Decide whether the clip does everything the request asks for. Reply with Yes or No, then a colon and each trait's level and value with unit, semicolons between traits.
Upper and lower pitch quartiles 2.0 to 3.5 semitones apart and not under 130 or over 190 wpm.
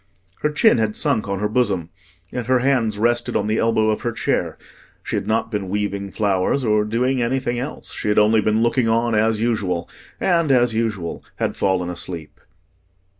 Yes: narrow, 2.6 semitones; average, 185 wpm